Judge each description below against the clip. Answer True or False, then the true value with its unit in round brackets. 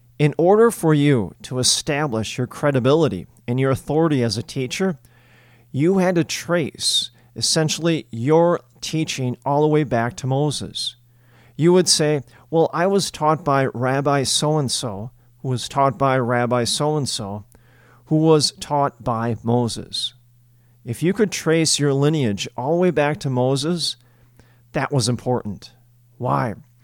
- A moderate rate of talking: True (150 wpm)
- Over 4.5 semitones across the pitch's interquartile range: False (4.2 semitones)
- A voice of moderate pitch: False (130 Hz)